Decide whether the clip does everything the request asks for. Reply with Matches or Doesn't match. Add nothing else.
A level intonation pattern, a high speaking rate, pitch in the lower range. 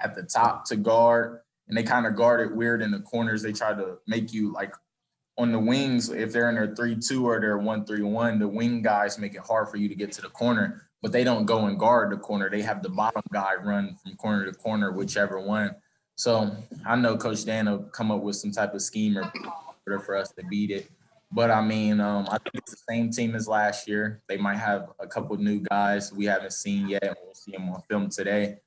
Matches